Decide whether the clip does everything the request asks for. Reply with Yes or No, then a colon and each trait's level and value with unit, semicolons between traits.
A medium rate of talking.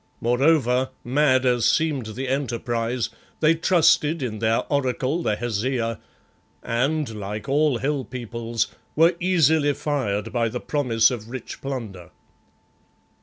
No: slow, 125 wpm